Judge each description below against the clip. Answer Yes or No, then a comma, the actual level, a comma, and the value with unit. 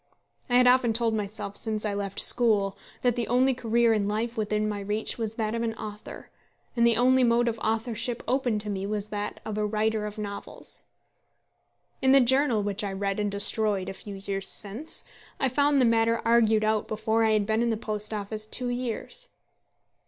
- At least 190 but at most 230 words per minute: Yes, average, 195 wpm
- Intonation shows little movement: Yes, narrow, 2.1 semitones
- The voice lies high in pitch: Yes, high, 220 Hz